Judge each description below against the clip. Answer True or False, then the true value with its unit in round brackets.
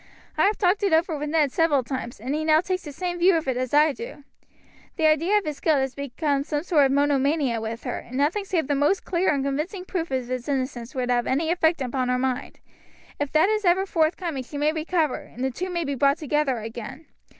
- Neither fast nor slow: False (240 wpm)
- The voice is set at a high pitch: True (295 Hz)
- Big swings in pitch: False (4.0 semitones)